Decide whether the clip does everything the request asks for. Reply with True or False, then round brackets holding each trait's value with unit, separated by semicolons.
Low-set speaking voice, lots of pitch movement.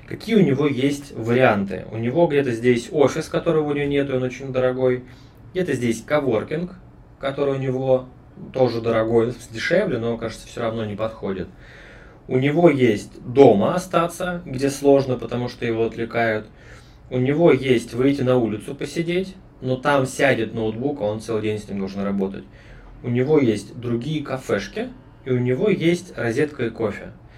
False (130 Hz; 3.7 semitones)